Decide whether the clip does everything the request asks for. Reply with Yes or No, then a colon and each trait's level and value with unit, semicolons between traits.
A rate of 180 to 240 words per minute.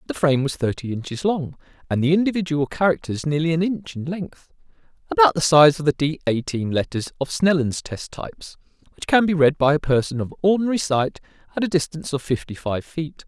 Yes: average, 195 wpm